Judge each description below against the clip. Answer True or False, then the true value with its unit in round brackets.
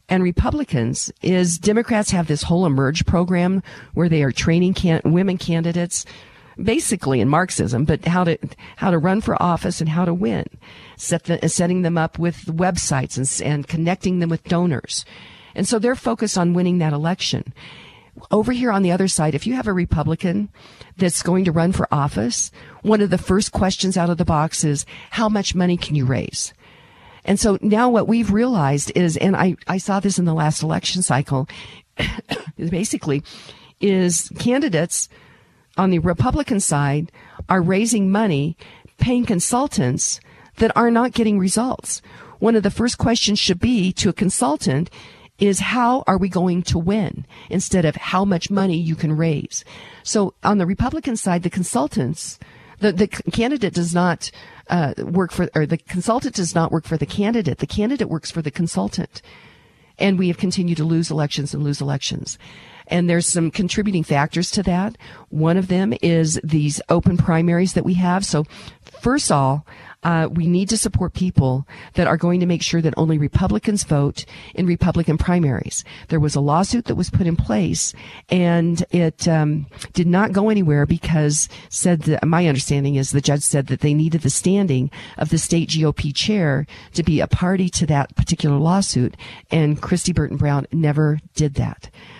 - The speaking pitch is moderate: True (175 Hz)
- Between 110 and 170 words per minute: False (180 wpm)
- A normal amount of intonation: True (3.9 semitones)